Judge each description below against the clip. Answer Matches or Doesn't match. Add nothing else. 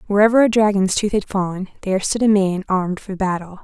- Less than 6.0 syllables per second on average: Doesn't match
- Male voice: Doesn't match